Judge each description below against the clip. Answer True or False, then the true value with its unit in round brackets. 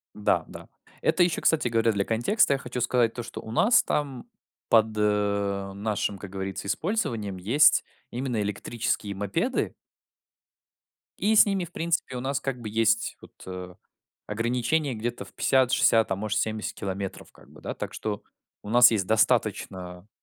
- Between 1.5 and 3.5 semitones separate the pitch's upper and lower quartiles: False (4.0 semitones)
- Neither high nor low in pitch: False (115 Hz)